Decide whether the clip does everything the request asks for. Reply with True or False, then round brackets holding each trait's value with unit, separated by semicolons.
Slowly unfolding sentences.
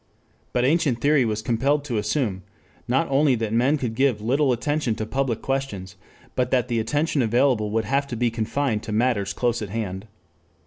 False (185 wpm)